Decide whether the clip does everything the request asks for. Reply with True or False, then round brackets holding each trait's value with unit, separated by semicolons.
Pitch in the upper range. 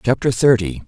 False (115 Hz)